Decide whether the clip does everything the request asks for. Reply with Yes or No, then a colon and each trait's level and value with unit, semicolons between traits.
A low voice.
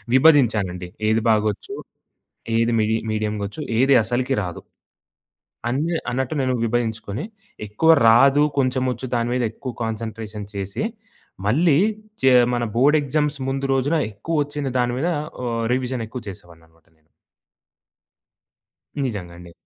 Yes: low, 120 Hz